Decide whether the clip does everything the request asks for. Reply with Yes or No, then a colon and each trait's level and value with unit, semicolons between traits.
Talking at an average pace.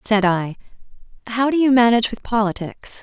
Yes: average, 160 wpm